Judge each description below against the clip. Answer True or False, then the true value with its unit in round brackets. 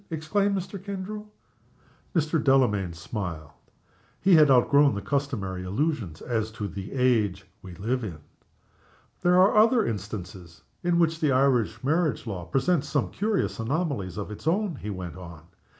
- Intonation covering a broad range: True (8.9 semitones)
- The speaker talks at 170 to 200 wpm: False (150 wpm)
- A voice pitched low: True (130 Hz)